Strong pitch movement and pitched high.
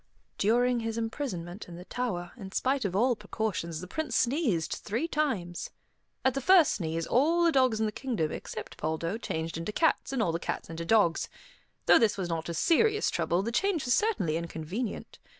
Yes: wide, 7.4 semitones; high, 220 Hz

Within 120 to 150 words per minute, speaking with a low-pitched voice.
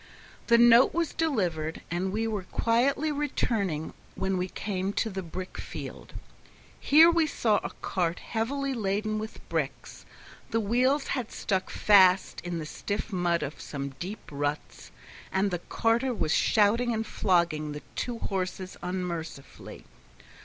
No: average, 145 wpm; high, 200 Hz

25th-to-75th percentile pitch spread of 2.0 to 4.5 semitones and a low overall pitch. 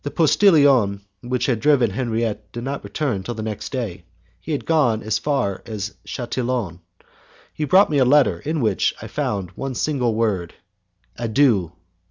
No: average, 5.1 semitones; low, 120 Hz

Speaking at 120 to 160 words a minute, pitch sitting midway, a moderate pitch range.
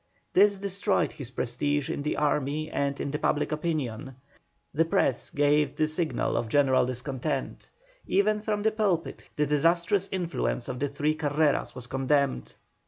Yes: average, 150 wpm; medium, 150 Hz; average, 3.7 semitones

